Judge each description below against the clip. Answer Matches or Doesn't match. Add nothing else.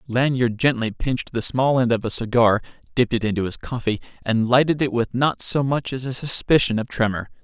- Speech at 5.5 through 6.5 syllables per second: Matches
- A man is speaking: Matches